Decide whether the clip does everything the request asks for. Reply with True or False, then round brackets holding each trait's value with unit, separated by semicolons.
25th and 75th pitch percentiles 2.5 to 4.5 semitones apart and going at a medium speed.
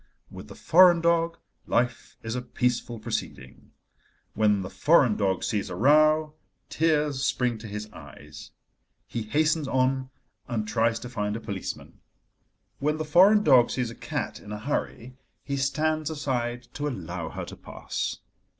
False (5.3 semitones; 155 wpm)